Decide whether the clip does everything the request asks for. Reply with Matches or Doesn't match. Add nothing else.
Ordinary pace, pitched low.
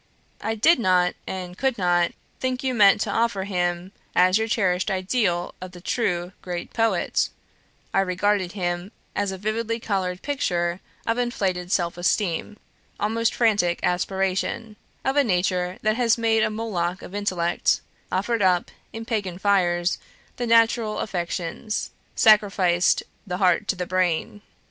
Doesn't match